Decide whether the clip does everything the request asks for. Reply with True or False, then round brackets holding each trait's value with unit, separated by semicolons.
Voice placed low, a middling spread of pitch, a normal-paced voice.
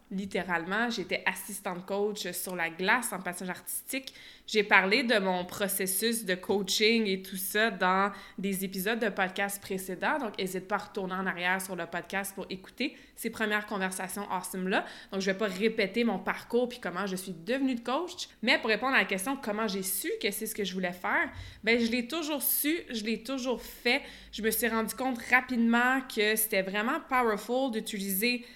False (210 Hz; 3.9 semitones; 195 wpm)